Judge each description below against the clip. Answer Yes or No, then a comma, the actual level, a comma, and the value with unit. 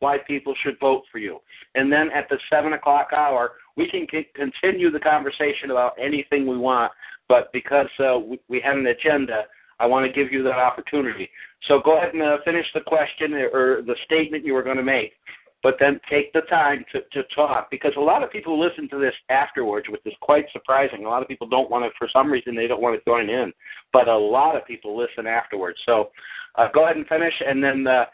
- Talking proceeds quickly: Yes, fast, 230 wpm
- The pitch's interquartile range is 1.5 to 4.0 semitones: Yes, average, 2.9 semitones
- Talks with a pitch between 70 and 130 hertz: No, medium, 140 Hz